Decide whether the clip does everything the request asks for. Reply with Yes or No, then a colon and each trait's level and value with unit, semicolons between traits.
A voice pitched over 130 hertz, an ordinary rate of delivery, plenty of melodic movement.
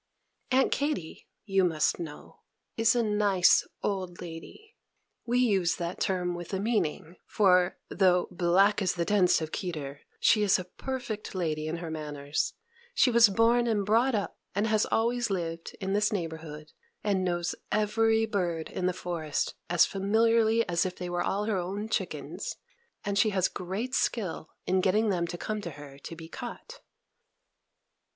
No: high, 190 Hz; average, 165 wpm; average, 4.1 semitones